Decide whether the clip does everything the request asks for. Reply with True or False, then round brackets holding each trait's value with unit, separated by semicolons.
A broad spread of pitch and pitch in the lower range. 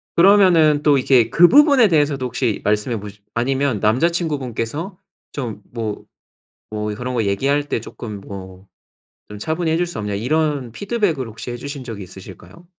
True (6.7 semitones; 130 Hz)